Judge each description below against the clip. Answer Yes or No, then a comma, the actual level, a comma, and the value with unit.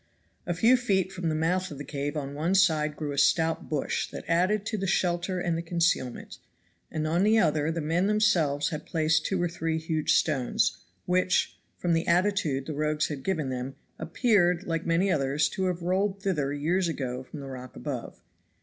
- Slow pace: No, average, 195 wpm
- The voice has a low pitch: No, medium, 165 Hz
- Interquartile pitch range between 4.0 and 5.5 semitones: No, average, 3.6 semitones